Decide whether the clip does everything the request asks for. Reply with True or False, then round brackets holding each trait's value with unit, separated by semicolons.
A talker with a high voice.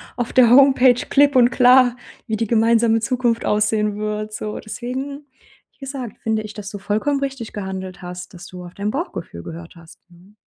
True (220 Hz)